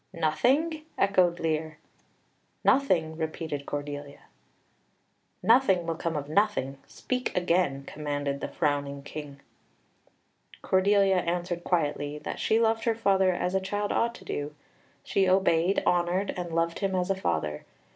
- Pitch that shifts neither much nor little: Yes, average, 4.7 semitones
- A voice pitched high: No, medium, 175 Hz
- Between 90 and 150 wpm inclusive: Yes, slow, 135 wpm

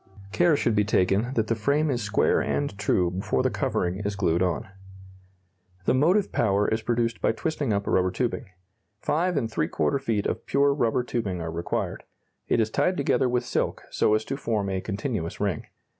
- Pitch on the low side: Yes, low, 110 Hz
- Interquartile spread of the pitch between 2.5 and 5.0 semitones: No, wide, 5.4 semitones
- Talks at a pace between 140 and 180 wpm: No, average, 190 wpm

